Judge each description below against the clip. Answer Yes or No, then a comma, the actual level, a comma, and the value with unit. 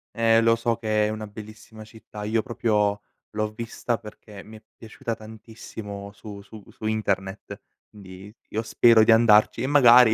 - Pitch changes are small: Yes, narrow, 1.4 semitones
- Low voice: Yes, low, 110 Hz